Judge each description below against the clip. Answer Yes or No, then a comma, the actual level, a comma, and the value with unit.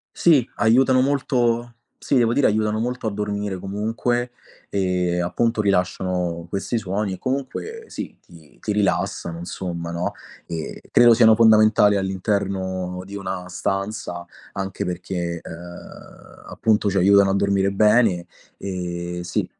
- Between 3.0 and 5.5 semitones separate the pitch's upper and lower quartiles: Yes, average, 3.7 semitones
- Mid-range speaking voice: No, low, 100 Hz